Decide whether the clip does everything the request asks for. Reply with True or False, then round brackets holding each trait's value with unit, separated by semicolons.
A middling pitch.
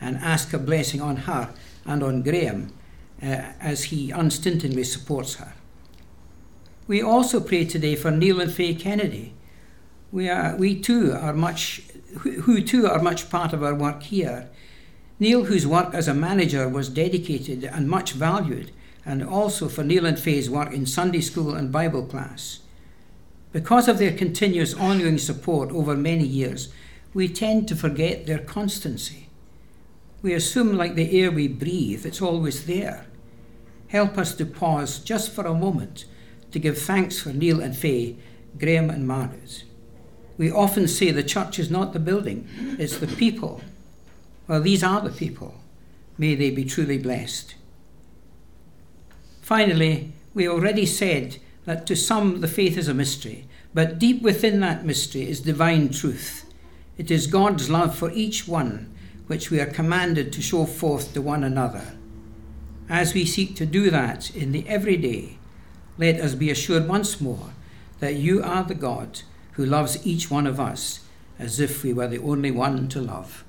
True (155 Hz)